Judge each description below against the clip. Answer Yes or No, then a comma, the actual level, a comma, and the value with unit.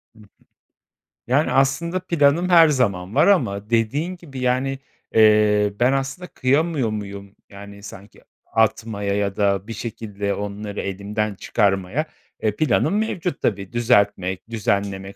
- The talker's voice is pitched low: Yes, low, 110 Hz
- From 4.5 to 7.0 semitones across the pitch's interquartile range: Yes, average, 5.1 semitones